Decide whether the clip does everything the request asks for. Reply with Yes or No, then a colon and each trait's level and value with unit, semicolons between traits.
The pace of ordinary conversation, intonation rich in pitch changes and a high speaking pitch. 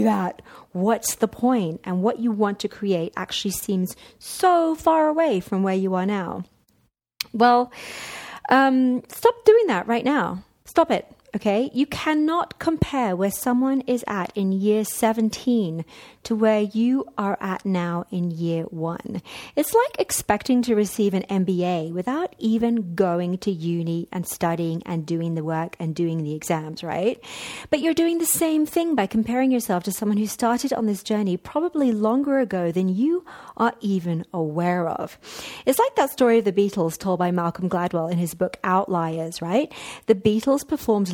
Yes: average, 170 wpm; wide, 5.9 semitones; high, 210 Hz